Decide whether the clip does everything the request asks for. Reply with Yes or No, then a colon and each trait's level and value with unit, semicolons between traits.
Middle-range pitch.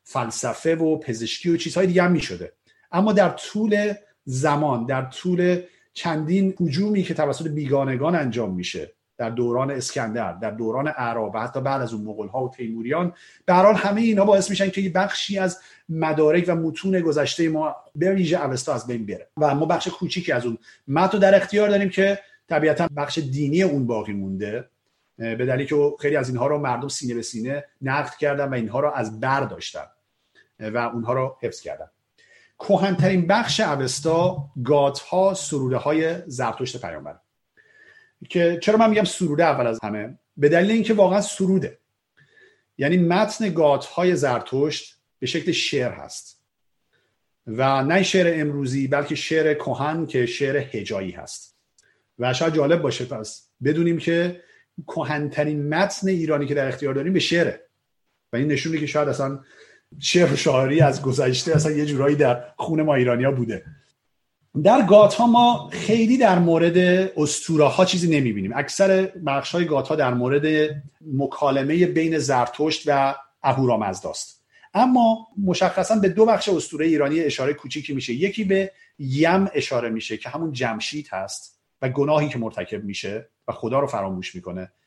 Yes: medium, 150 Hz